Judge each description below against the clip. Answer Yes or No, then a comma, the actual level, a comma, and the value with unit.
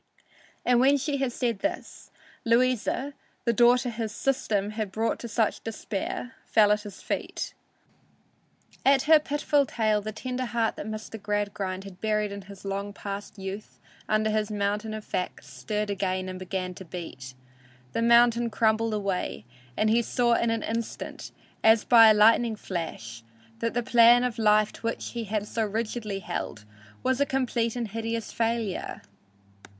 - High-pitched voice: Yes, high, 220 Hz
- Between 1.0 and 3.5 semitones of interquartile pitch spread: Yes, average, 2.7 semitones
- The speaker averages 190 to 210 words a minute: No, average, 165 wpm